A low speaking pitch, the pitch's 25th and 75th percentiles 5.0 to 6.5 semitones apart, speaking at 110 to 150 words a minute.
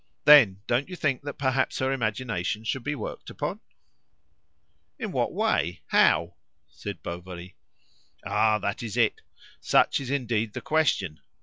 Yes: low, 115 Hz; wide, 5.5 semitones; average, 140 wpm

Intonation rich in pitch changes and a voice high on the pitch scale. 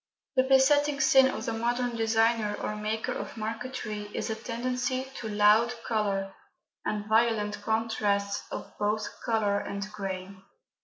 No: narrow, 2.4 semitones; high, 220 Hz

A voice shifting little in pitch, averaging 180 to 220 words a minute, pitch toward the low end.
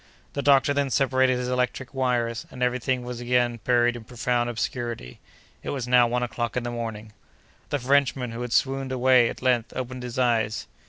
Yes: narrow, 1.4 semitones; average, 195 wpm; low, 125 Hz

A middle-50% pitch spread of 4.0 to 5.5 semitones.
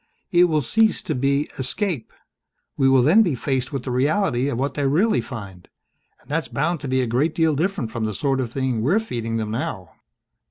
Yes: average, 4.7 semitones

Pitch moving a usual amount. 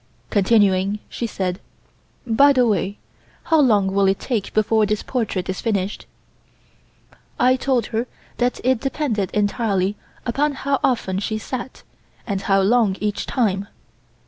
Yes: average, 4.1 semitones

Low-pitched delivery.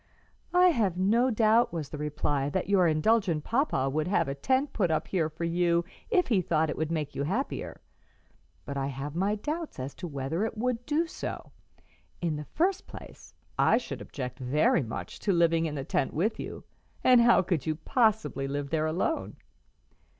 No: medium, 170 Hz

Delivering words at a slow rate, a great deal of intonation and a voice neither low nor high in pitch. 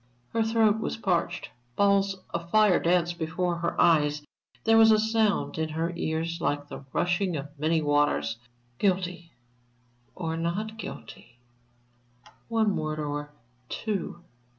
No: slow, 130 wpm; average, 4.4 semitones; medium, 175 Hz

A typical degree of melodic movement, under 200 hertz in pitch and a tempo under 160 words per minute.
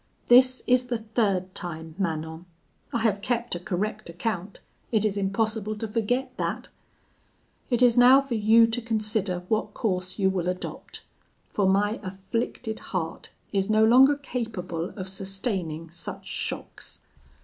No: average, 3.8 semitones; high, 210 Hz; average, 145 wpm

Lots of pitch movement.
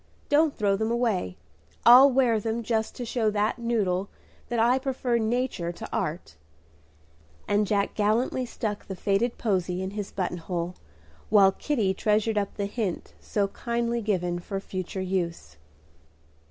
No: average, 3.8 semitones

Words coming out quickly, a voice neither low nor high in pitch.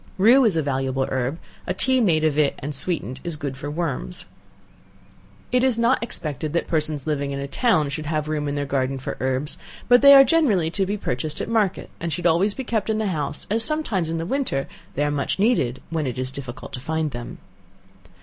Yes: fast, 220 wpm; medium, 155 Hz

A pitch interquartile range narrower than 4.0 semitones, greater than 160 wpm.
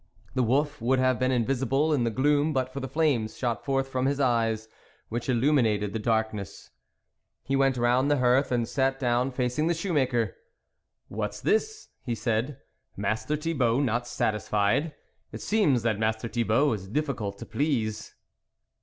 Yes: average, 3.6 semitones; average, 175 wpm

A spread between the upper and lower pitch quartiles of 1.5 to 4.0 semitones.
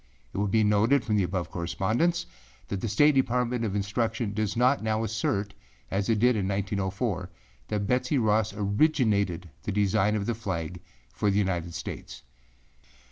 Yes: average, 2.8 semitones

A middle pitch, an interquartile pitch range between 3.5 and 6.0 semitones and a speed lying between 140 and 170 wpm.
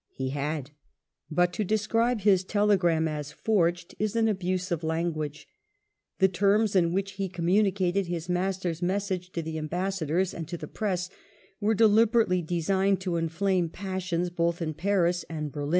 No: medium, 180 Hz; average, 2.9 semitones; average, 160 wpm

